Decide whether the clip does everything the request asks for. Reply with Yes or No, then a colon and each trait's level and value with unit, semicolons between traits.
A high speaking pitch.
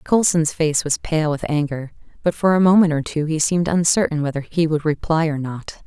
No: medium, 160 Hz